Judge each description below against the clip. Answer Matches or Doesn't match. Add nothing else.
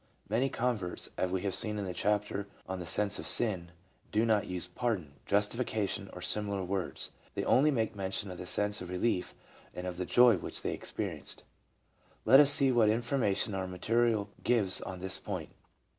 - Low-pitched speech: Matches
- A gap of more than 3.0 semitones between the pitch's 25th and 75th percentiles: Matches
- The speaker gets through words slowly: Doesn't match